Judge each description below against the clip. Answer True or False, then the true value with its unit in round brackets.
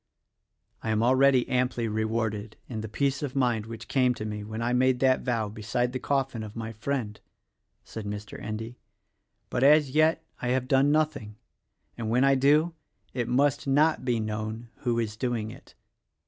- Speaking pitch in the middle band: False (120 Hz)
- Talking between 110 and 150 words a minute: False (175 wpm)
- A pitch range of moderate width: True (3.5 semitones)